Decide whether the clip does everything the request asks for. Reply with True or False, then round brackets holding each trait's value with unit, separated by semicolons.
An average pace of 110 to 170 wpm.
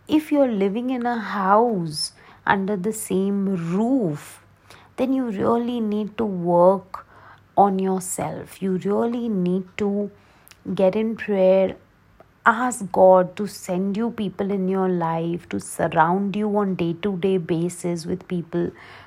True (140 wpm)